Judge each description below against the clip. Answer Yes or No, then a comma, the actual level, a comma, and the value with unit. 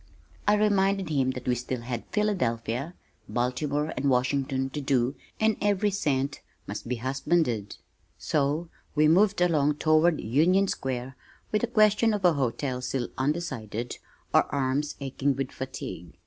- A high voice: No, medium, 140 Hz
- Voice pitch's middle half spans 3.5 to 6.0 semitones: Yes, wide, 5.4 semitones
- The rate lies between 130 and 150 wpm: Yes, average, 145 wpm